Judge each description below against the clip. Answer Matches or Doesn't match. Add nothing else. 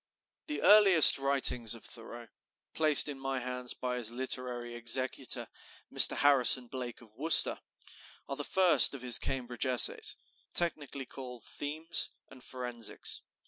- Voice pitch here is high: Doesn't match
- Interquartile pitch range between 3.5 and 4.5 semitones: Doesn't match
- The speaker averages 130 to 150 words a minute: Matches